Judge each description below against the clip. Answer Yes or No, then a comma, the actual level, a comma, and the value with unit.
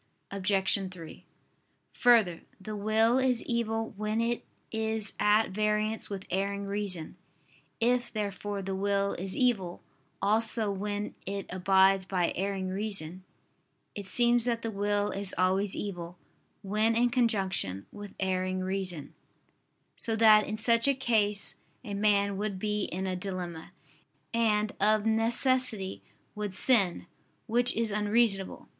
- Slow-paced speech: Yes, slow, 130 wpm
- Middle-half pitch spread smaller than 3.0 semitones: Yes, narrow, 2.6 semitones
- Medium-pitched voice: No, high, 205 Hz